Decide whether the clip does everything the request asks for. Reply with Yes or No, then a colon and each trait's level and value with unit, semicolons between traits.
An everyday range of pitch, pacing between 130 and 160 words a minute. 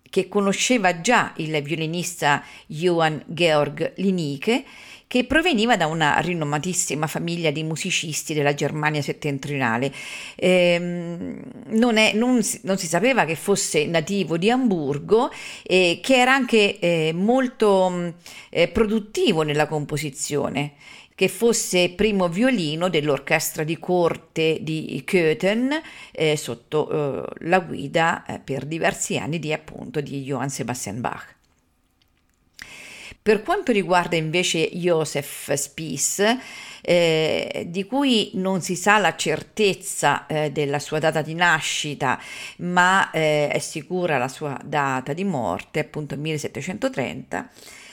No: average, 4.6 semitones; average, 120 wpm